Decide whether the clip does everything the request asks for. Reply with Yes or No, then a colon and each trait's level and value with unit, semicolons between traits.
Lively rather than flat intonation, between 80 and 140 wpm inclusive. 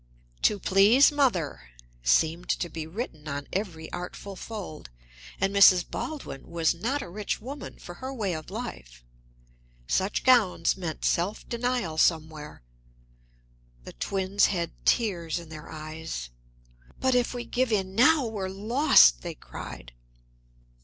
Yes: wide, 6.2 semitones; slow, 135 wpm